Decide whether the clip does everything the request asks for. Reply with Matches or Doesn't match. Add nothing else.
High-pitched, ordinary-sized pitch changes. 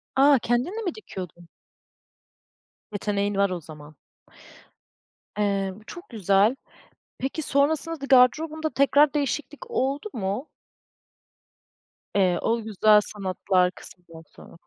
Doesn't match